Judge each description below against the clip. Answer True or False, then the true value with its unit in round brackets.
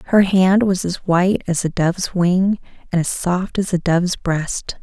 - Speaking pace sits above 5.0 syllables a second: False (4.5 syllables/s)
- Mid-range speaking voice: True (180 Hz)